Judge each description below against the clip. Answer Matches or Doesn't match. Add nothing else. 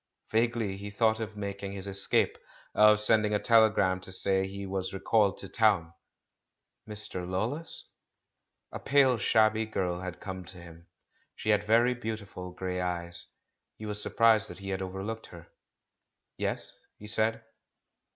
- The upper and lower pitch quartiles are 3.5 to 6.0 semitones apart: Doesn't match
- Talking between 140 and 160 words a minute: Matches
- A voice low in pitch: Matches